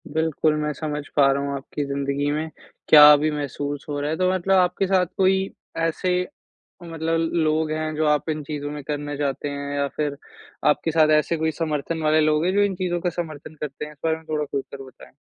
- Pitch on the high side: No, medium, 155 Hz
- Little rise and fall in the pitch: Yes, narrow, 2.1 semitones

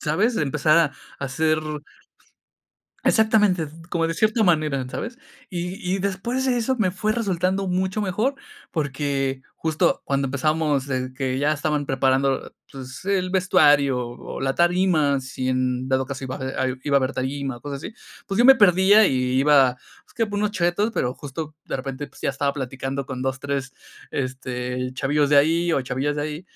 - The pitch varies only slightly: No, wide, 5.5 semitones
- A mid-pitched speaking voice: Yes, medium, 145 Hz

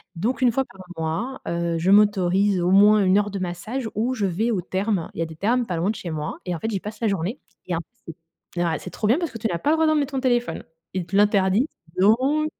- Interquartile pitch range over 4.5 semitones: Yes, average, 5.0 semitones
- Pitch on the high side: Yes, high, 205 Hz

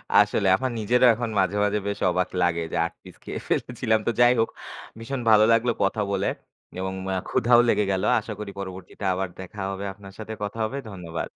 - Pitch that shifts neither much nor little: Yes, average, 3.2 semitones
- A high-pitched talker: No, low, 105 Hz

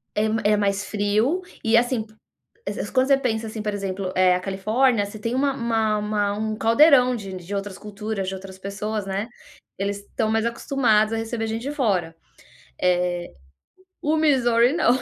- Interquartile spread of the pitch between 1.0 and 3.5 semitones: Yes, average, 2.9 semitones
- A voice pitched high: Yes, high, 215 Hz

